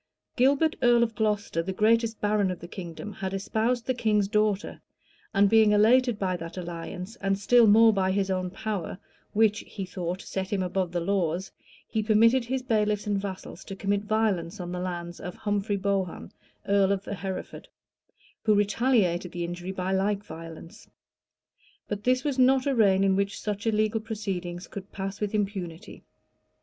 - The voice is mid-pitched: No, high, 200 Hz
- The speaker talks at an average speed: Yes, average, 170 wpm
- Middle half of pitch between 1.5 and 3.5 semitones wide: Yes, average, 2.7 semitones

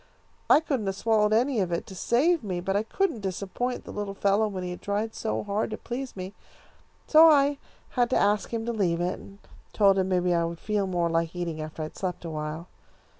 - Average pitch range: Yes, average, 4.1 semitones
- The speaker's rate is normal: No, fast, 225 wpm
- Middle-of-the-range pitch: No, high, 200 Hz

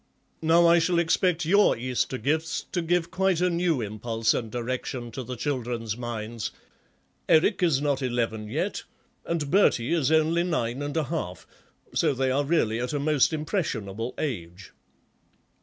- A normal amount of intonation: No, wide, 5.8 semitones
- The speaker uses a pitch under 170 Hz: Yes, medium, 140 Hz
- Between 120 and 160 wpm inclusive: Yes, average, 155 wpm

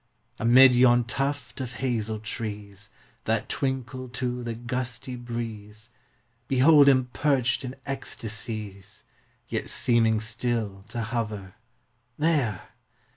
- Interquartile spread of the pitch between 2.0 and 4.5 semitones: Yes, average, 3.0 semitones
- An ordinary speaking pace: No, slow, 105 wpm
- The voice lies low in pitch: Yes, low, 120 Hz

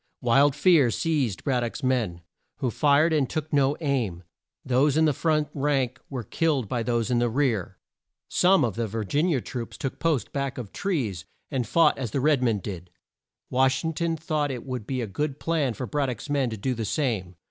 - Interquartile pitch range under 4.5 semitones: Yes, average, 4.1 semitones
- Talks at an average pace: No, fast, 215 wpm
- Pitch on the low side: Yes, low, 130 Hz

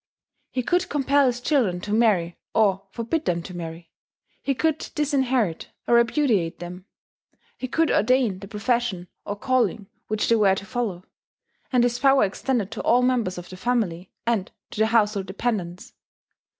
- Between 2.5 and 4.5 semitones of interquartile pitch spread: No, average, 5.1 semitones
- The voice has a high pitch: Yes, high, 225 Hz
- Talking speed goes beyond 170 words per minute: No, average, 165 wpm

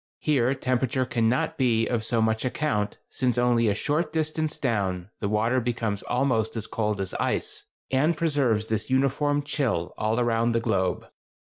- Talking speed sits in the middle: Yes, average, 160 wpm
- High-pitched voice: No, low, 120 Hz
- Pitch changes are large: No, average, 3.4 semitones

